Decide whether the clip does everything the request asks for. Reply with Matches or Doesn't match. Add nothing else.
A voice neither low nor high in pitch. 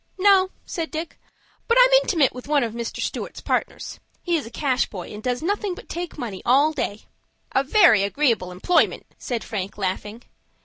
Doesn't match